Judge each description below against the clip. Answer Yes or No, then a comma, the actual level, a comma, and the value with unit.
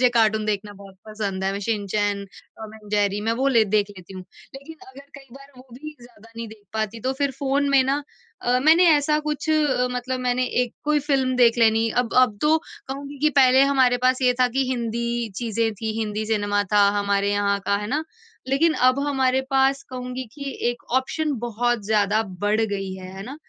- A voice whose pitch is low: No, high, 240 Hz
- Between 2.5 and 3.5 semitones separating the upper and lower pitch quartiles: No, average, 4.2 semitones